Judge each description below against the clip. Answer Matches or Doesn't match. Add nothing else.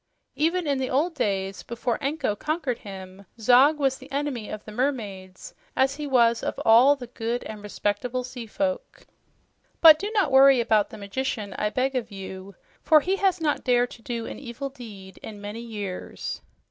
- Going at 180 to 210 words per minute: Matches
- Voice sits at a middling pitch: Doesn't match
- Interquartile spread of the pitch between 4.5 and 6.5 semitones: Matches